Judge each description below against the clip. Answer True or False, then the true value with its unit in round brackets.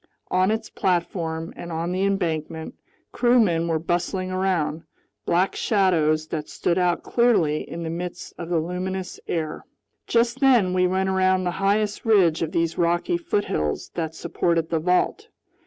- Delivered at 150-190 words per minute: True (155 wpm)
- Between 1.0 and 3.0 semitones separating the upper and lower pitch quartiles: True (2.7 semitones)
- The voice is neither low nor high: True (180 Hz)